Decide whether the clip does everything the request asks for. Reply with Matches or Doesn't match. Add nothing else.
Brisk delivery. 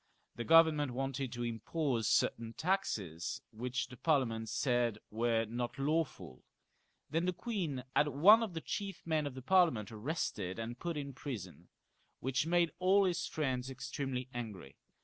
Doesn't match